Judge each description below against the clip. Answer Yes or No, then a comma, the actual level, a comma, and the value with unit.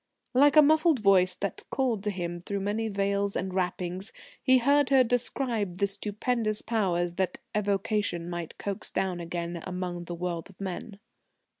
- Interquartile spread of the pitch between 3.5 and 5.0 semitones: Yes, average, 3.9 semitones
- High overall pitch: Yes, high, 200 Hz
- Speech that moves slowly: No, average, 160 wpm